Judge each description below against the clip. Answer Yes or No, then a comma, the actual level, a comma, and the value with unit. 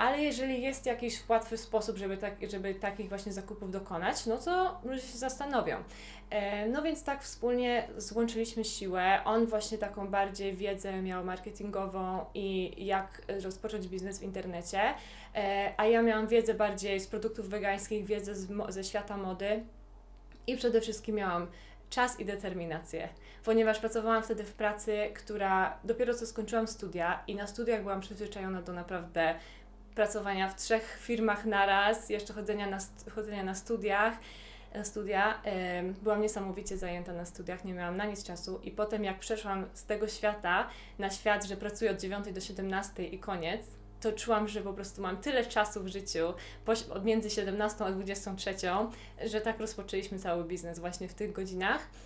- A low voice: No, high, 205 Hz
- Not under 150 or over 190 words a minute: Yes, fast, 160 wpm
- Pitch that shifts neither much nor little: No, narrow, 2.3 semitones